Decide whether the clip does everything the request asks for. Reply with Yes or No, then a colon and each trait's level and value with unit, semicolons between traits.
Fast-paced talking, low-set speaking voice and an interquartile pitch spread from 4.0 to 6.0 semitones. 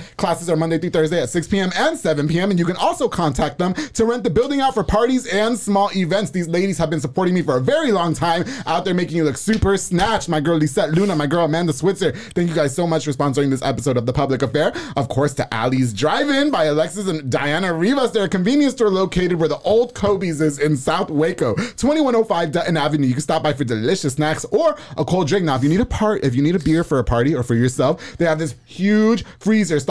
No: fast, 255 wpm; medium, 170 Hz; average, 4.9 semitones